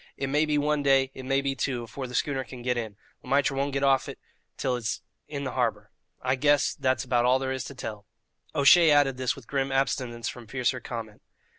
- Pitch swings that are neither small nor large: No, narrow, 2.0 semitones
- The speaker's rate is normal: No, fast, 235 wpm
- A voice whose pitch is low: Yes, low, 130 Hz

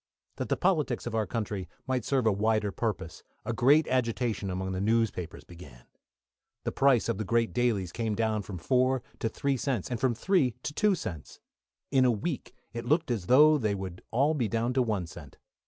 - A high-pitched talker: No, low, 115 Hz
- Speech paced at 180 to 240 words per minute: Yes, average, 200 wpm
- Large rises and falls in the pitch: No, average, 4.4 semitones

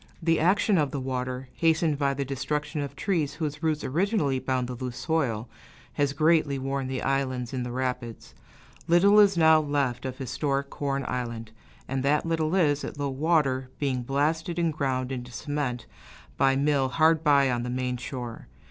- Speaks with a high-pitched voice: No, medium, 140 Hz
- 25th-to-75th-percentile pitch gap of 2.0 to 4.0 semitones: Yes, average, 3.4 semitones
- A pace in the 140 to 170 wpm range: No, average, 180 wpm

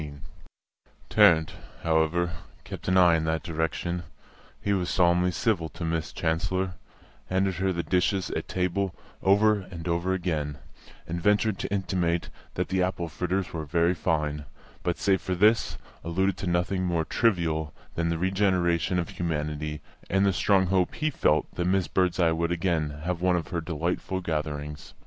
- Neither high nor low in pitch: No, very low, 85 Hz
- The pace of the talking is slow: No, average, 165 wpm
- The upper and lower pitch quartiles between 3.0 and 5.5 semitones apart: No, narrow, 2.5 semitones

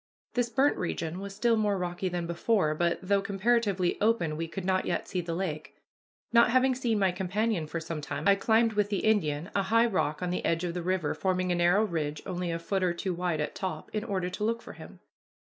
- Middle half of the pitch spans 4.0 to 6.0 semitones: No, average, 3.6 semitones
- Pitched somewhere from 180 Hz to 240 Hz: Yes, medium, 185 Hz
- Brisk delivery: Yes, fast, 230 wpm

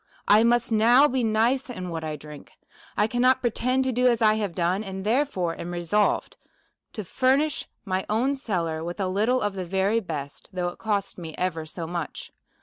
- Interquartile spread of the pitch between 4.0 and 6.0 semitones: Yes, wide, 5.4 semitones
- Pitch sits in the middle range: No, high, 205 Hz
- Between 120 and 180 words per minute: No, average, 195 wpm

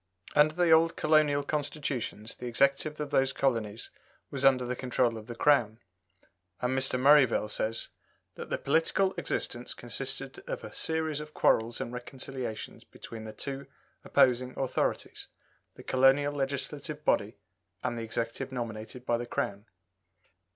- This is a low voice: Yes, low, 130 Hz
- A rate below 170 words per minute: Yes, average, 145 wpm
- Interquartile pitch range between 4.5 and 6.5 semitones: No, average, 3.8 semitones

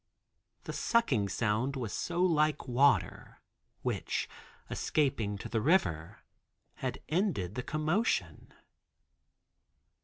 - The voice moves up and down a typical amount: No, wide, 7.6 semitones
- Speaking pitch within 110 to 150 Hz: Yes, low, 135 Hz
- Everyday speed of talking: No, slow, 95 wpm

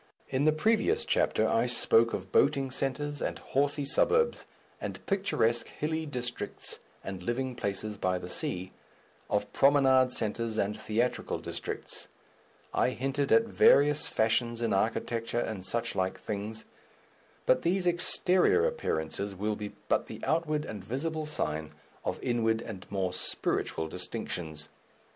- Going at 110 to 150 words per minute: Yes, slow, 135 wpm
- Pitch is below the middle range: Yes, low, 120 Hz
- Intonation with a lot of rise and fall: Yes, wide, 6.5 semitones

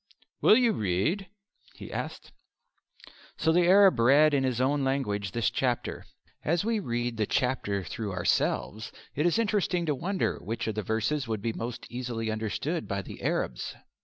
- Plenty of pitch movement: Yes, wide, 6.6 semitones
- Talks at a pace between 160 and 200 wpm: Yes, average, 165 wpm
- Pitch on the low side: Yes, low, 125 Hz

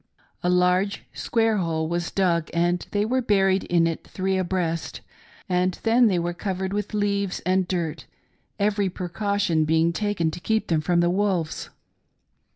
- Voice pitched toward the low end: No, medium, 185 Hz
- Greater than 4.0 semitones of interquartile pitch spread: No, average, 2.9 semitones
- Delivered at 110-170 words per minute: Yes, average, 160 wpm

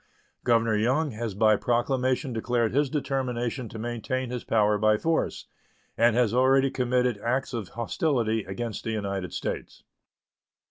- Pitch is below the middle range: Yes, low, 120 Hz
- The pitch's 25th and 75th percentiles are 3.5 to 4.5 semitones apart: No, average, 2.8 semitones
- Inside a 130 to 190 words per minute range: Yes, average, 140 wpm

